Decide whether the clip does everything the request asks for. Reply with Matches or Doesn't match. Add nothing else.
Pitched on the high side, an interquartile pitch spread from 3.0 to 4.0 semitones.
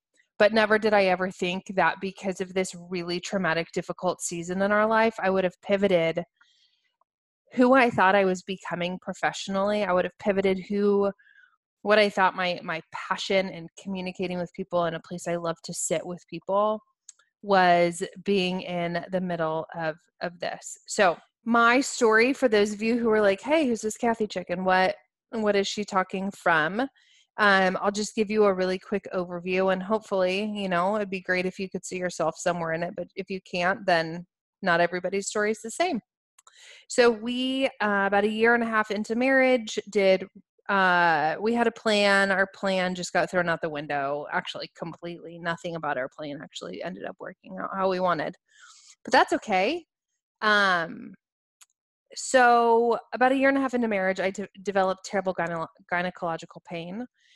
Matches